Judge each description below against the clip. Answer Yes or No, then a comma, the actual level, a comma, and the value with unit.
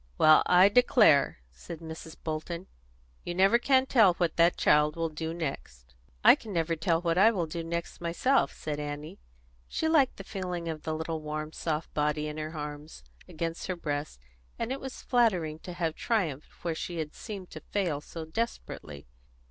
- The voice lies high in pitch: No, medium, 165 Hz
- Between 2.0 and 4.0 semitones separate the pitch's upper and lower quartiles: Yes, average, 3.2 semitones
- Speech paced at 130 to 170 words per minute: No, average, 180 wpm